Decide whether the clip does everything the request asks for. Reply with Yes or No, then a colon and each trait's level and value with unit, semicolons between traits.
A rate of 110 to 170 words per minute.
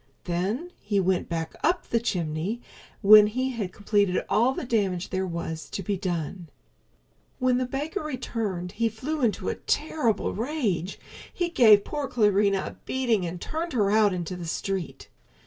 Yes: average, 165 wpm